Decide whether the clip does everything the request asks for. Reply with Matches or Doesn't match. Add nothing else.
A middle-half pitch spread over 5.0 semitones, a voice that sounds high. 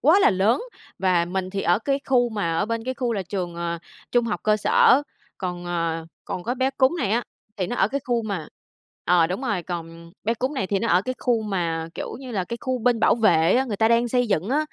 Matches